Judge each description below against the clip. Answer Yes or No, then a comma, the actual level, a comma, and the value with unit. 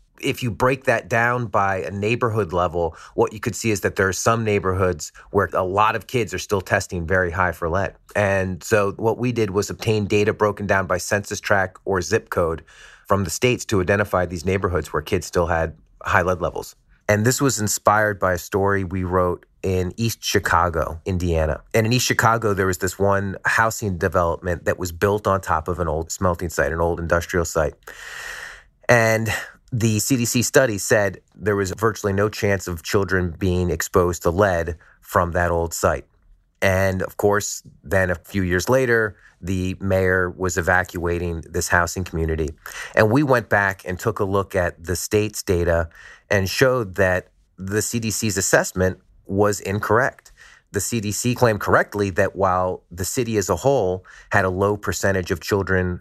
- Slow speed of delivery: No, average, 180 wpm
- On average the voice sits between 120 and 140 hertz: No, very low, 95 Hz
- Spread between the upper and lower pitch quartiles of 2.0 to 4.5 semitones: Yes, average, 2.7 semitones